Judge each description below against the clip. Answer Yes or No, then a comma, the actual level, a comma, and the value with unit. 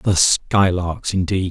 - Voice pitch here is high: No, very low, 90 Hz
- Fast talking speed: No, slow, 120 wpm